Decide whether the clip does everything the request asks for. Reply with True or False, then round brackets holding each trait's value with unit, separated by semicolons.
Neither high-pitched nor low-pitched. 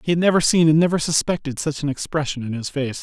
True (150 Hz)